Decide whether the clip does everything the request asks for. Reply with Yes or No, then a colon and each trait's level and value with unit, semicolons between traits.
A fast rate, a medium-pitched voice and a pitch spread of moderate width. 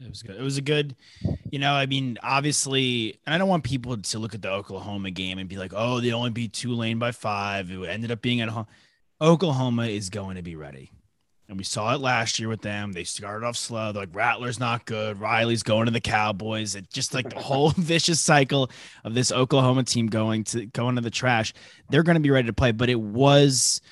No: fast, 235 wpm; low, 115 Hz; average, 3.7 semitones